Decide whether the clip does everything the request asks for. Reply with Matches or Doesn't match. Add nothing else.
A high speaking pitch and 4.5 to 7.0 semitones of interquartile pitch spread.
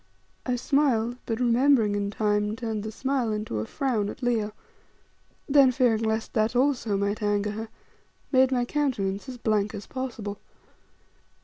Doesn't match